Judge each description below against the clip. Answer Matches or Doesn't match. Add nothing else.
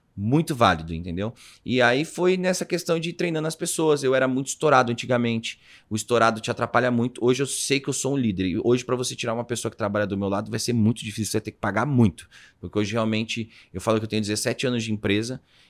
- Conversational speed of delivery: Doesn't match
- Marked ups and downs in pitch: Doesn't match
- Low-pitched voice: Matches